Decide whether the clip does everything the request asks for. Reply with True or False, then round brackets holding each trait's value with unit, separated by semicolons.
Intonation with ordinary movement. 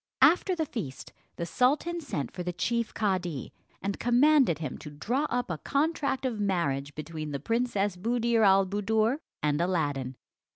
False (7.3 semitones)